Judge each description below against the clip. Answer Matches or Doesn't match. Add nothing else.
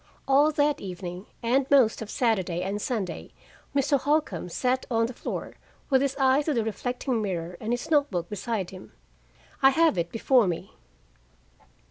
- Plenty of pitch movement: Matches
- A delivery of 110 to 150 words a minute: Doesn't match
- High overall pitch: Matches